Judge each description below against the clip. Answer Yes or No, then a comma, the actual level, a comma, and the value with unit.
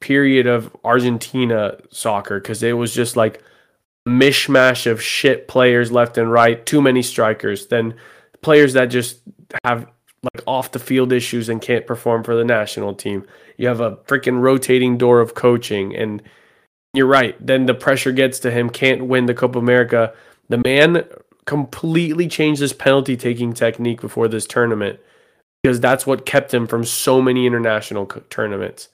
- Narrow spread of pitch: Yes, narrow, 2.2 semitones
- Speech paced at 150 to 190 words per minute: Yes, average, 170 wpm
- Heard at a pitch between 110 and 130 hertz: Yes, low, 125 Hz